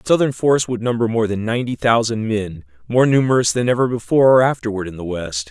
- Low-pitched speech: Yes, low, 115 Hz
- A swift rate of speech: Yes, fast, 220 wpm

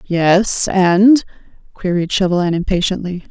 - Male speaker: No, female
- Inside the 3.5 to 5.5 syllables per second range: Yes, 4.1 syllables/s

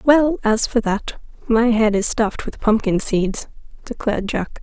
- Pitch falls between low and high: No, high, 220 Hz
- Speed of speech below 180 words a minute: Yes, average, 170 wpm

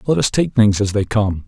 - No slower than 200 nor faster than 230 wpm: No, fast, 285 wpm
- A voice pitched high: No, low, 110 Hz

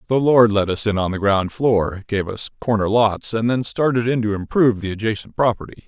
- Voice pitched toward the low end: Yes, low, 110 Hz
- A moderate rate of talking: No, fast, 225 wpm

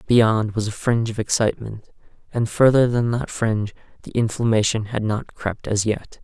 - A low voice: Yes, low, 110 Hz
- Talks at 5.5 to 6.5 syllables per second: No, 5.1 syllables/s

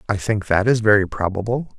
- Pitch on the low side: Yes, low, 105 Hz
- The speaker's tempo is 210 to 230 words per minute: No, average, 200 wpm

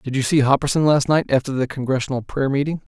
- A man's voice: Yes, male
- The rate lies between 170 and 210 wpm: No, fast, 225 wpm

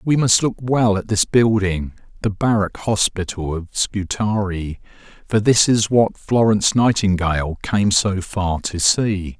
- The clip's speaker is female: No, male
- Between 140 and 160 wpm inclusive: Yes, average, 145 wpm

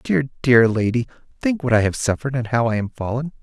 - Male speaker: Yes, male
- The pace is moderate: No, fast, 230 wpm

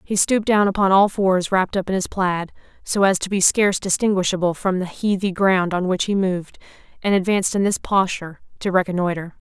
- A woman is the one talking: Yes, female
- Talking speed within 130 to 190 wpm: No, fast, 205 wpm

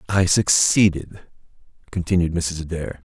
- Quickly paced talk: No, slow, 95 wpm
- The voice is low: Yes, very low, 85 Hz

